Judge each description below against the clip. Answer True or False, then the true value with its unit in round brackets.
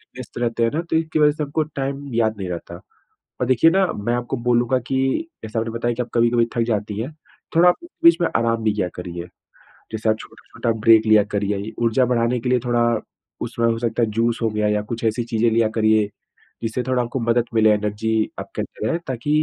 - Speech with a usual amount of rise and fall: False (2.3 semitones)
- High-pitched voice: False (115 Hz)